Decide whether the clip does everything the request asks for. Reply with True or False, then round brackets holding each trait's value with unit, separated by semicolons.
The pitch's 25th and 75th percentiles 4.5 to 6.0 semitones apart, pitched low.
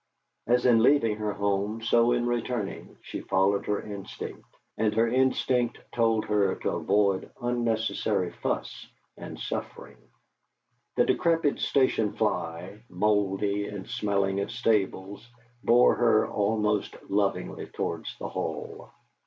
False (2.8 semitones; 105 Hz)